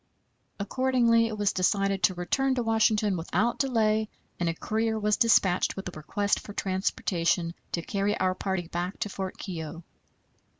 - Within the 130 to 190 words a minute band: Yes, average, 160 wpm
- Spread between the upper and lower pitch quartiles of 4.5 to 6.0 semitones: No, average, 3.5 semitones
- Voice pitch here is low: No, high, 200 Hz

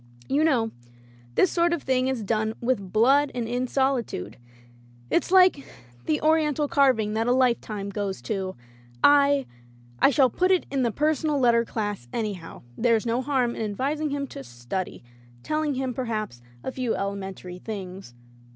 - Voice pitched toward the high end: Yes, high, 240 Hz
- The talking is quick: No, average, 170 wpm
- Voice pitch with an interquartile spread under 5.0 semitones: No, wide, 5.4 semitones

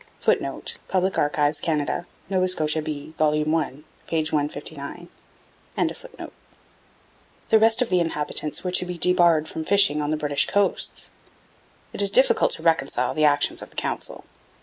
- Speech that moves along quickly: No, average, 150 wpm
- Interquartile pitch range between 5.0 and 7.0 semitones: No, average, 3.4 semitones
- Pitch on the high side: No, medium, 160 Hz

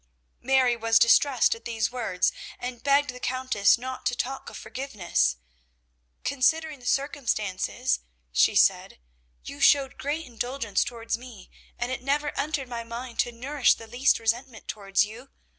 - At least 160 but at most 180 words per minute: No, average, 150 wpm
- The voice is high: Yes, high, 245 Hz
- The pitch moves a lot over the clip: No, average, 3.0 semitones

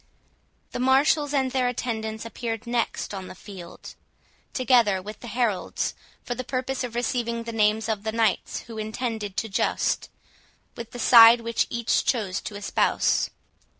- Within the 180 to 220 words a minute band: No, average, 155 wpm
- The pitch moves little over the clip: Yes, narrow, 2.3 semitones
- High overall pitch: Yes, high, 230 Hz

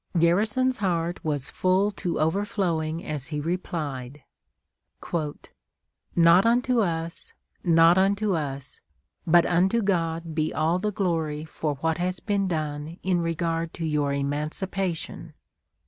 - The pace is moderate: No, slow, 120 wpm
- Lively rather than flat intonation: No, average, 3.3 semitones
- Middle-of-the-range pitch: Yes, medium, 170 Hz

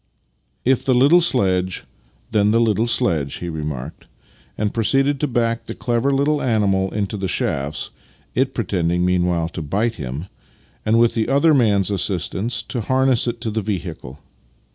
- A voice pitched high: No, low, 105 Hz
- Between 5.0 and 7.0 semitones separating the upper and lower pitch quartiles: Yes, average, 5.3 semitones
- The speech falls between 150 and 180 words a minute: Yes, average, 165 wpm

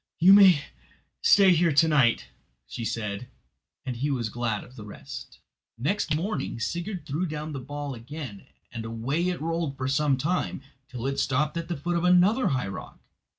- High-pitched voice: No, medium, 145 Hz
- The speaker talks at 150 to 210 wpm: Yes, average, 180 wpm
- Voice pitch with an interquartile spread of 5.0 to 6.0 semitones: Yes, wide, 5.5 semitones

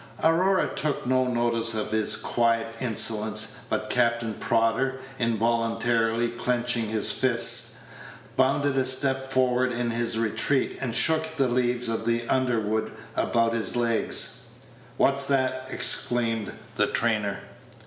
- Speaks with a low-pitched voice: Yes, low, 120 Hz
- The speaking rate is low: Yes, slow, 125 wpm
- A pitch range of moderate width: No, narrow, 2.3 semitones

